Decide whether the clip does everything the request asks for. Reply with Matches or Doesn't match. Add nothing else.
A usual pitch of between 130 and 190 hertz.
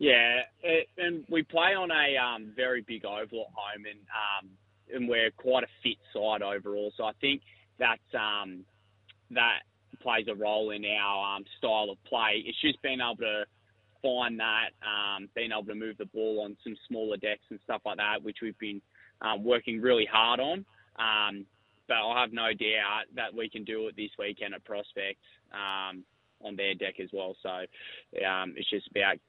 Doesn't match